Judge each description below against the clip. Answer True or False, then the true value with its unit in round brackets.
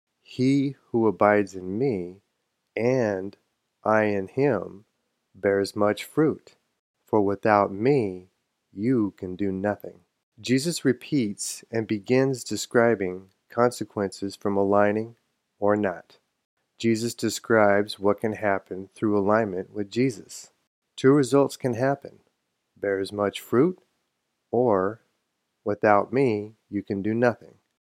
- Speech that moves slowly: True (110 wpm)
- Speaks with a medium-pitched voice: False (105 Hz)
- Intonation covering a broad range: False (3.1 semitones)